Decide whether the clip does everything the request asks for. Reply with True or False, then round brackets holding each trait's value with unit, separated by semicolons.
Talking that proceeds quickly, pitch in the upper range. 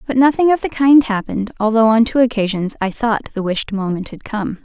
True (220 wpm; 225 Hz)